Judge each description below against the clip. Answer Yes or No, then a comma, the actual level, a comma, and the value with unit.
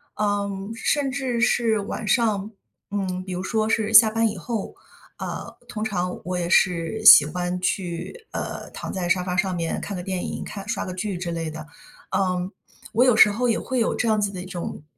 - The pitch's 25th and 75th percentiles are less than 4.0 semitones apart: Yes, average, 3.5 semitones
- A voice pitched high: Yes, high, 195 Hz